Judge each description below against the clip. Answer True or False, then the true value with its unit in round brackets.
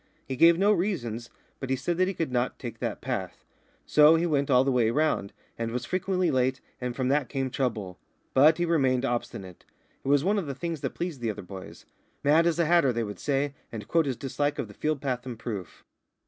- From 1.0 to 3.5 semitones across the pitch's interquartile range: False (5.1 semitones)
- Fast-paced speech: True (230 wpm)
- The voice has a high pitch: False (135 Hz)